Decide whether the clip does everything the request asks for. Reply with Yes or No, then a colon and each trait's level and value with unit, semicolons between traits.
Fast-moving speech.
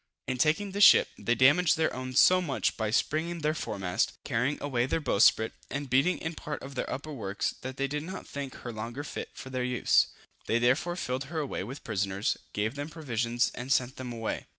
Yes: fast, 210 wpm